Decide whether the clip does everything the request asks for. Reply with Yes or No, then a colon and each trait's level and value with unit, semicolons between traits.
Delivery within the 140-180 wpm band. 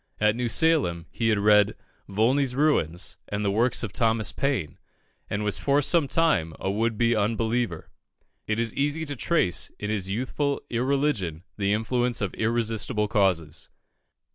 Yes: average, 155 wpm